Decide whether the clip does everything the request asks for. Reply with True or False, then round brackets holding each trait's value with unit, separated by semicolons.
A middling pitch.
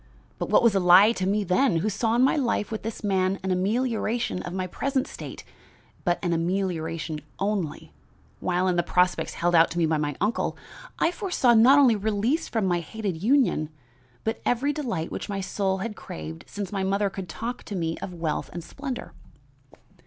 False (195 Hz)